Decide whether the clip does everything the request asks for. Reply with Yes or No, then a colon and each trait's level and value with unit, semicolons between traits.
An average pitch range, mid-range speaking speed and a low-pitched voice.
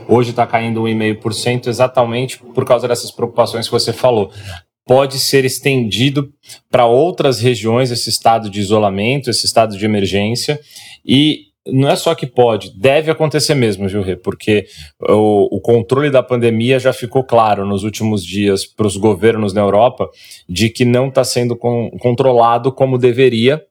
Yes: average, 3.4 semitones; average, 155 wpm; low, 120 Hz